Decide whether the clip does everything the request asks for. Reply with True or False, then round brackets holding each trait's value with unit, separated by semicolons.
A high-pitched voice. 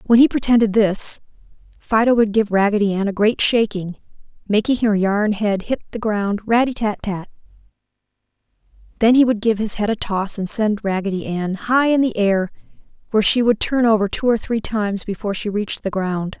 True (210 Hz)